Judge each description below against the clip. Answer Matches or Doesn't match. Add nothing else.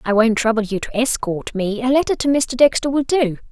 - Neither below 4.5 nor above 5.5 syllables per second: Matches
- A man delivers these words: Doesn't match